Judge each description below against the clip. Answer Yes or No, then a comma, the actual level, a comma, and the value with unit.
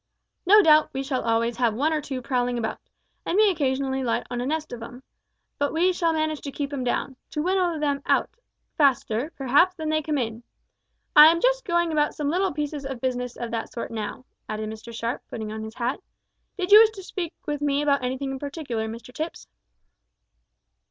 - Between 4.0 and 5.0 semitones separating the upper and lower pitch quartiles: Yes, average, 4.4 semitones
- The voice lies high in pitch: Yes, very high, 280 Hz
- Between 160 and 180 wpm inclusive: No, fast, 205 wpm